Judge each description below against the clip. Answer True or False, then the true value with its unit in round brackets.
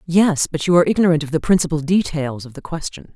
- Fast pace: True (230 wpm)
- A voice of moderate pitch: True (160 Hz)